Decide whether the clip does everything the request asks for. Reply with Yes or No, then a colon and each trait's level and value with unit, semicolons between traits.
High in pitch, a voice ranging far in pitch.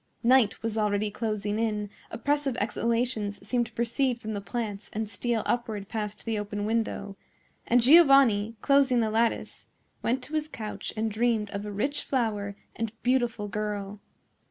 No: high, 225 Hz; average, 2.7 semitones